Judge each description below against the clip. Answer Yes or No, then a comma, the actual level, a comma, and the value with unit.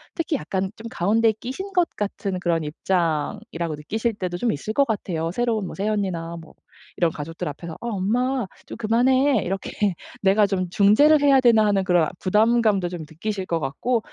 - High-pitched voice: Yes, high, 200 Hz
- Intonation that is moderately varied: Yes, average, 4.9 semitones